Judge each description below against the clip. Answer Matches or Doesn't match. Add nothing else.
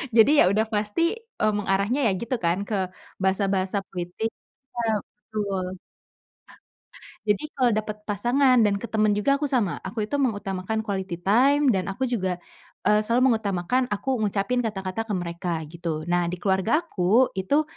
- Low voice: Doesn't match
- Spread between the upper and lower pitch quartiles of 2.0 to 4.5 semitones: Matches